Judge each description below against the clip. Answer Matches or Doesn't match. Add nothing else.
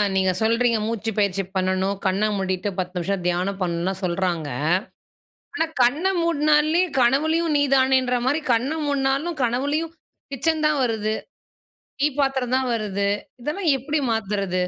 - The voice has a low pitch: Doesn't match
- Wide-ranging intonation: Matches